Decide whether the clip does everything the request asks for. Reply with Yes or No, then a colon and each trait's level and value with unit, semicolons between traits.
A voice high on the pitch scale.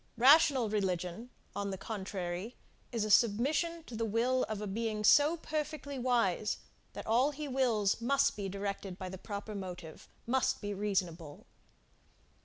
Yes: high, 215 Hz